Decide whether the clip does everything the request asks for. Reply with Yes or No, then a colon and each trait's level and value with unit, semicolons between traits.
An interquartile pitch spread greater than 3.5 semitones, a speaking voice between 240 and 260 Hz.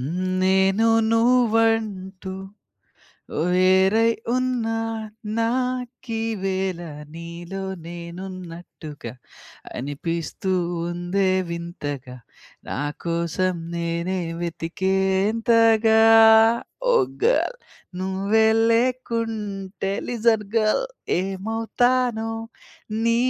No: average, 4.4 semitones; high, 195 Hz